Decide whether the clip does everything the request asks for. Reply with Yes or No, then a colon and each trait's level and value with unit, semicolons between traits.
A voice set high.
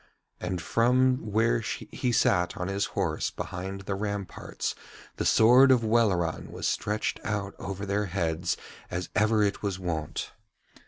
No: low, 100 Hz